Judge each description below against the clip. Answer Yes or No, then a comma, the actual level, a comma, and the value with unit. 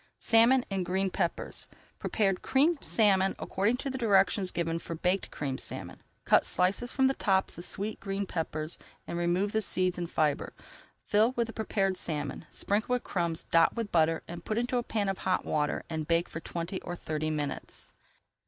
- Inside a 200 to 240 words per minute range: No, average, 175 wpm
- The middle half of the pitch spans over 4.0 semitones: Yes, average, 4.6 semitones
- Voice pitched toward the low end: No, high, 190 Hz